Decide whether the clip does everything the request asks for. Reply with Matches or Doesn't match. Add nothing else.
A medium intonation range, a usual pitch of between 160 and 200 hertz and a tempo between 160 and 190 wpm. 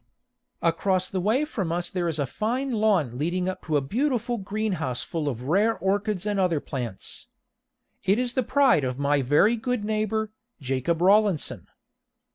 Doesn't match